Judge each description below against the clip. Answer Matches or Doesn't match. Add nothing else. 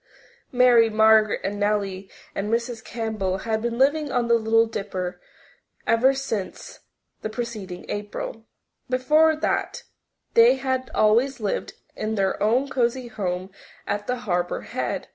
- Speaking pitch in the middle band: Doesn't match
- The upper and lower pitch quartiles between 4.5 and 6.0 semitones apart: Doesn't match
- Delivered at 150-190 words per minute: Doesn't match